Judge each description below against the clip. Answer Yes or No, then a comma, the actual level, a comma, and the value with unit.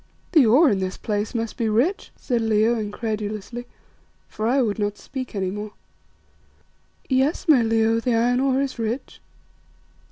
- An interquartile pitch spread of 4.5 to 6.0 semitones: No, average, 3.2 semitones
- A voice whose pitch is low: No, high, 225 Hz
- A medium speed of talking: Yes, average, 155 wpm